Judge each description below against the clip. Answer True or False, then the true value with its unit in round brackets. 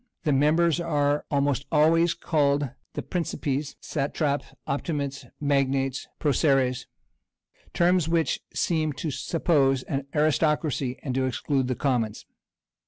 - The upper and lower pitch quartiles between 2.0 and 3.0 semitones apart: True (2.6 semitones)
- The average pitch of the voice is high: False (145 Hz)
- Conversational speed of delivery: False (110 wpm)